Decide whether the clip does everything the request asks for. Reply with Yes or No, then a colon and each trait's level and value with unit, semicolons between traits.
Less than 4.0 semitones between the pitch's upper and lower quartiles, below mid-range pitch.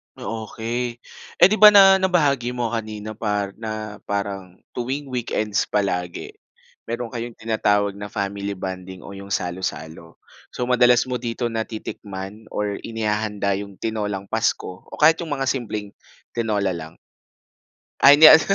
Yes: average, 3.4 semitones; low, 110 Hz